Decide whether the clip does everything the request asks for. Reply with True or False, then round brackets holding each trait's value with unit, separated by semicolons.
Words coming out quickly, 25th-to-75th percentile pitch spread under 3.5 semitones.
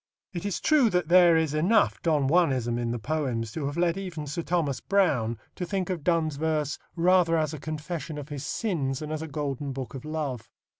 False (210 wpm; 3.9 semitones)